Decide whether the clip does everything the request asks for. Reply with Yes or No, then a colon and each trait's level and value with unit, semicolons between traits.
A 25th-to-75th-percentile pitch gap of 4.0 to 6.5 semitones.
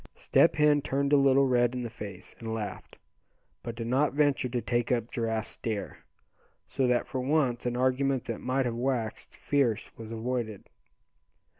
No: average, 2.8 semitones